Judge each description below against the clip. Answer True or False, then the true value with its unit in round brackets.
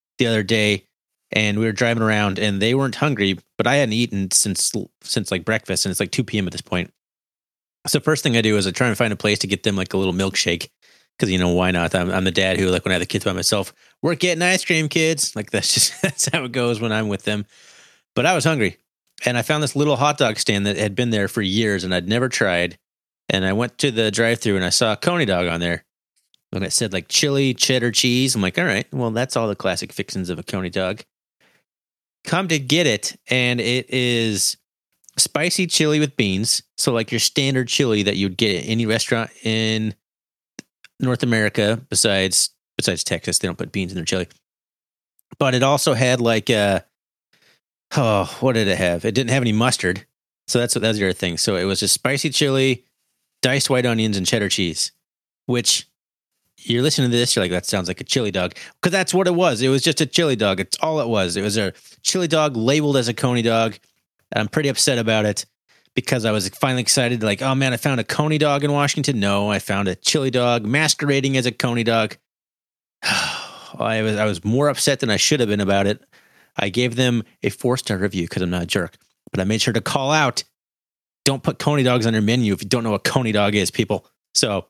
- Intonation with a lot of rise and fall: False (4.7 semitones)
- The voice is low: True (115 Hz)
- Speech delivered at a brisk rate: True (230 wpm)